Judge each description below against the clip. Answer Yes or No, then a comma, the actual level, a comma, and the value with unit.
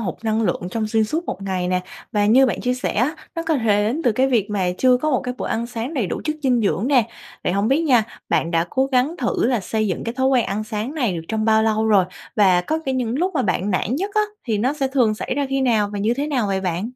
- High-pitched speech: Yes, high, 230 Hz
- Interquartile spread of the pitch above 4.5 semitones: No, average, 4.2 semitones